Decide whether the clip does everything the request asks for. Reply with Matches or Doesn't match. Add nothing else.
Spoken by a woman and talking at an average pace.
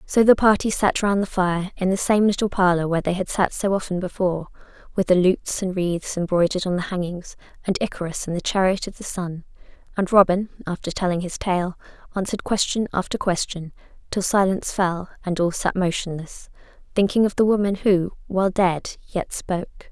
Matches